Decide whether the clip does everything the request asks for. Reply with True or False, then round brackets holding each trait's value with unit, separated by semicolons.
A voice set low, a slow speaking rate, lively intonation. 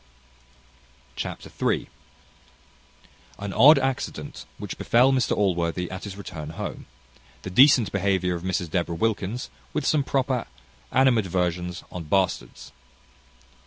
True (95 Hz; 115 wpm; 5.9 semitones)